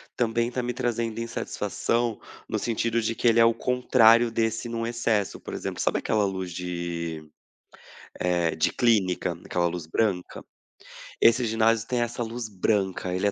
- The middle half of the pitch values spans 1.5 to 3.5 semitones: No, average, 4.2 semitones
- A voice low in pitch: Yes, low, 115 Hz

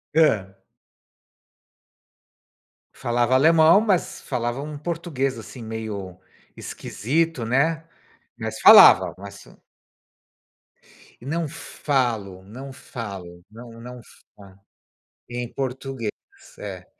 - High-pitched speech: No, low, 125 Hz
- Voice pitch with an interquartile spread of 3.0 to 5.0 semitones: No, wide, 5.5 semitones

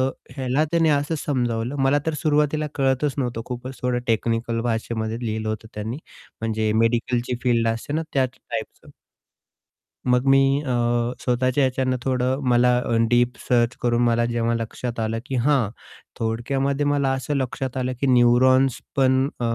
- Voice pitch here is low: Yes, low, 125 Hz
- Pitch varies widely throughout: No, narrow, 2.4 semitones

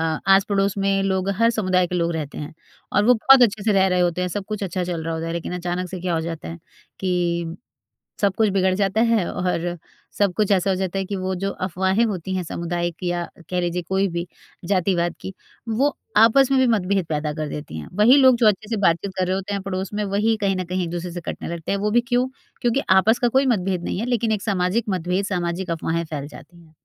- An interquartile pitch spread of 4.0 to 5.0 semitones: No, average, 2.9 semitones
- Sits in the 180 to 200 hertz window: Yes, high, 190 Hz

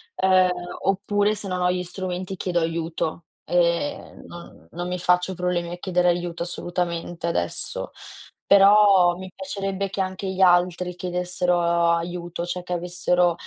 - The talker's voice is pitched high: No, medium, 180 Hz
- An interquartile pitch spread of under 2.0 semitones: Yes, narrow, 1.3 semitones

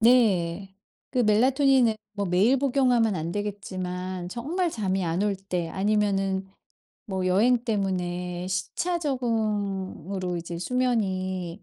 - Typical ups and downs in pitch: Yes, average, 4.4 semitones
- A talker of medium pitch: No, high, 195 Hz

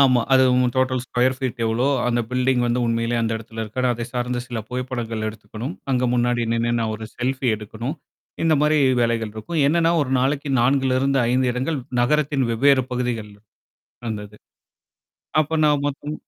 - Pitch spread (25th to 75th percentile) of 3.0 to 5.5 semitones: No, narrow, 2.6 semitones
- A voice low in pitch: Yes, low, 125 Hz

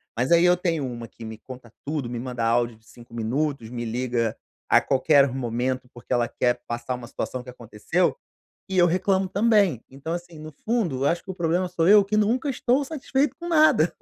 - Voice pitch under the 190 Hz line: Yes, medium, 140 Hz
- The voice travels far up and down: Yes, wide, 7.5 semitones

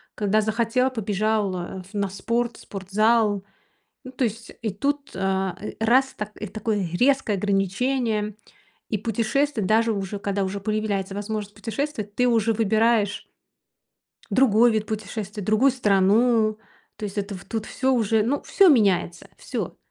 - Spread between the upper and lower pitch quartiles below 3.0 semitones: Yes, narrow, 2.6 semitones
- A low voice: No, high, 215 Hz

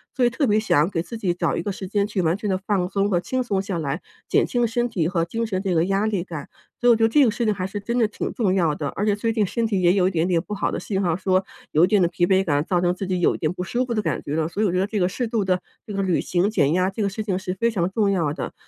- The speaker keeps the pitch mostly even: No, average, 3.3 semitones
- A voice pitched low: No, high, 190 Hz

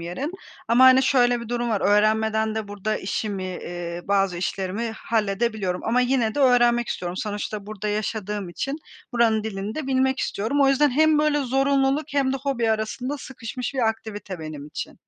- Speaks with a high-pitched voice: Yes, high, 220 Hz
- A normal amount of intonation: Yes, average, 4.3 semitones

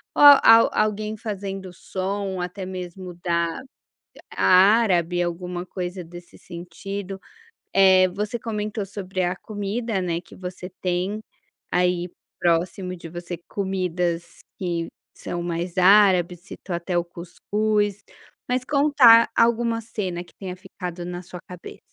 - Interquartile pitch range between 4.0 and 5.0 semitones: No, average, 2.7 semitones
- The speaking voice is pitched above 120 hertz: Yes, medium, 185 Hz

